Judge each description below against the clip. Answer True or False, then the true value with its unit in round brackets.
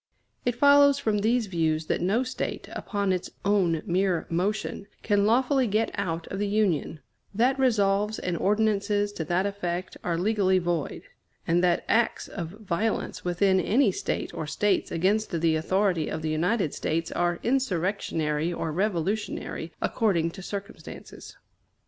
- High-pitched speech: True (195 Hz)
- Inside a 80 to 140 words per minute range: False (150 wpm)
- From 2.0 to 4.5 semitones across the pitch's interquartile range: True (3.9 semitones)